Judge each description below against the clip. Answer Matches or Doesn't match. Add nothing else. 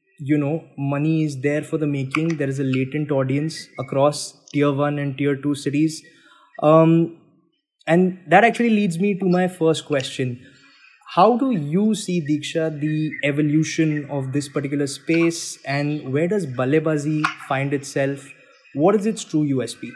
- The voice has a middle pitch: Matches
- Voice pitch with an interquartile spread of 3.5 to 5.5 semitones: Doesn't match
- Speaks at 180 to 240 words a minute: Doesn't match